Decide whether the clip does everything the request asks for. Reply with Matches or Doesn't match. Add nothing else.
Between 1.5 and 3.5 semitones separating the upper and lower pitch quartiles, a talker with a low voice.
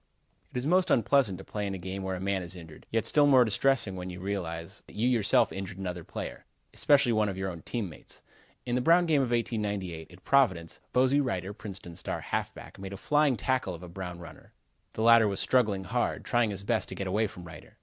Doesn't match